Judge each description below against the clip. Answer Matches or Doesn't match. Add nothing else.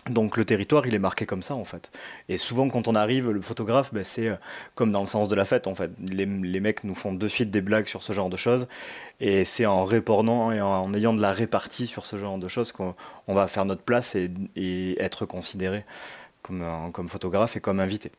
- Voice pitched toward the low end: Matches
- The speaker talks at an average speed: Doesn't match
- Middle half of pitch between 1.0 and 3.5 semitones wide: Matches